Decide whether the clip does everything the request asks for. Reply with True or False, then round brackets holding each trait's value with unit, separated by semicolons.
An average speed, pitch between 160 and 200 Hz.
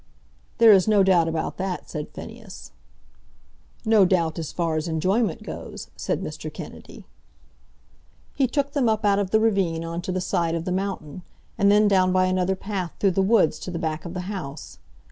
True (190 wpm; 185 Hz)